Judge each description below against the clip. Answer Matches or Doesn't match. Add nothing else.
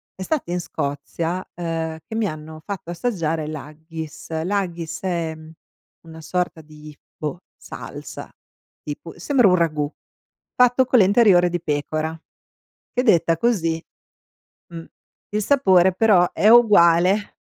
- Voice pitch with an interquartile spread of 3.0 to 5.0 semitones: Matches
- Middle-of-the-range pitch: Matches